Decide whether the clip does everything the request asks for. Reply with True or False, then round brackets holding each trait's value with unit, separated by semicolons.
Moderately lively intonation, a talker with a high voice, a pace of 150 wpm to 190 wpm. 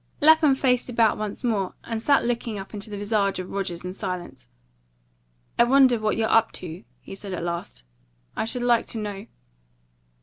True (3.6 semitones; 215 Hz; 180 wpm)